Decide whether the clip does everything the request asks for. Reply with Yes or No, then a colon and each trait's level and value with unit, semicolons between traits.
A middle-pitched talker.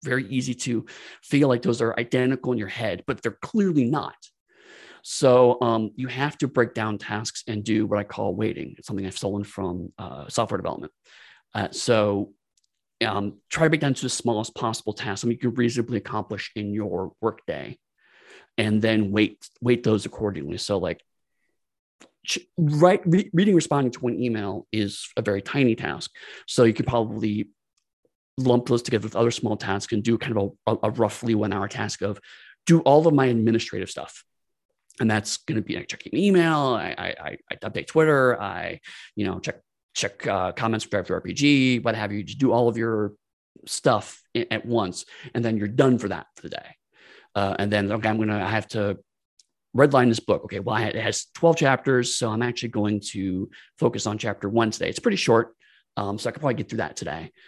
No: low, 115 Hz